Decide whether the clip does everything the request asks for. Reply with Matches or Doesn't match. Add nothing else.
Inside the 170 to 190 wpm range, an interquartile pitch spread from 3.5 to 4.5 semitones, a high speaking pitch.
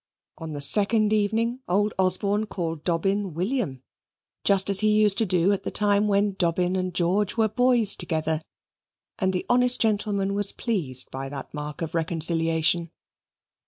Doesn't match